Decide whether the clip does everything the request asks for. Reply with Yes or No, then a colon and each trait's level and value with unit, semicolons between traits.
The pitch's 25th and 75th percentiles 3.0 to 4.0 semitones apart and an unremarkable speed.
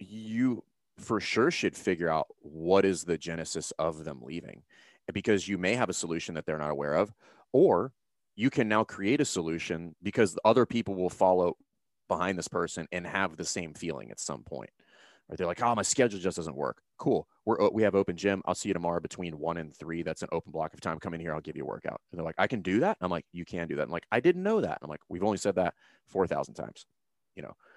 No: average, 3.5 semitones; fast, 255 wpm